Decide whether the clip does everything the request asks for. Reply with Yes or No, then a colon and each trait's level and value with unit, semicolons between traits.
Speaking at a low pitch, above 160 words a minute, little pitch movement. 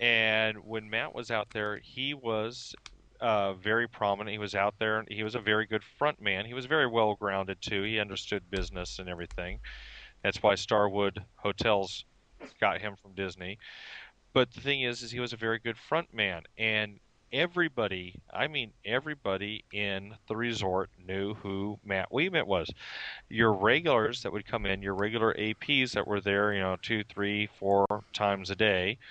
Yes: low, 105 Hz; average, 175 wpm; narrow, 2.3 semitones